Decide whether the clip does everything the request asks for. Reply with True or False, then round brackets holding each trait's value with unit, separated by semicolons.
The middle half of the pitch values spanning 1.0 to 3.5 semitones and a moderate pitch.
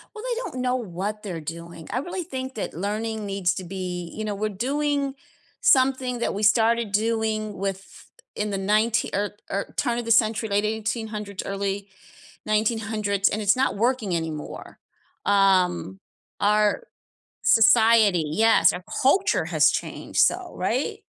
False (2.9 semitones; 215 Hz)